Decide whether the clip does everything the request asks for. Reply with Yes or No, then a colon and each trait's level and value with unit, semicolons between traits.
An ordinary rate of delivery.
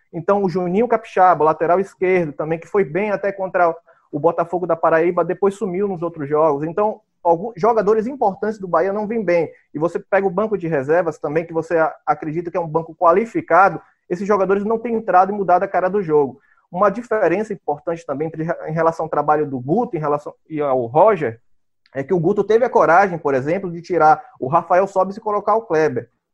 No: fast, 205 wpm